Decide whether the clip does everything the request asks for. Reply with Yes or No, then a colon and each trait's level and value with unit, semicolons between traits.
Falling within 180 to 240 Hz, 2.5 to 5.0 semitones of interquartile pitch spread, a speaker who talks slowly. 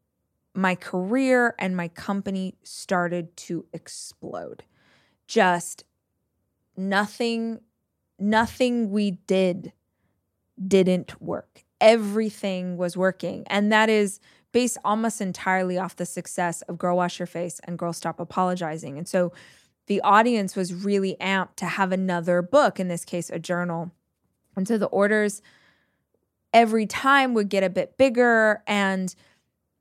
Yes: high, 190 Hz; average, 3.2 semitones; slow, 130 wpm